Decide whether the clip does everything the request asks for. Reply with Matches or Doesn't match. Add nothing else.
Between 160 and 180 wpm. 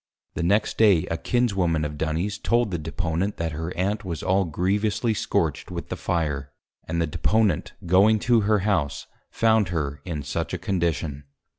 Matches